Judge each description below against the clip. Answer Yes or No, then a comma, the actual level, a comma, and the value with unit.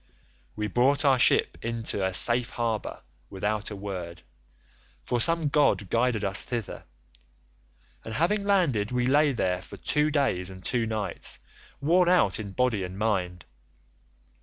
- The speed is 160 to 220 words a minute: No, average, 145 wpm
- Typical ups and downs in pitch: No, wide, 5.9 semitones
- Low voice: Yes, low, 115 Hz